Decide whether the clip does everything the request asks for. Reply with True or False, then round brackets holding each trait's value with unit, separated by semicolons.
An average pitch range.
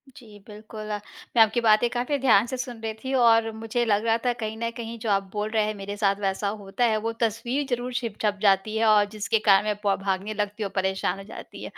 False (2.1 semitones)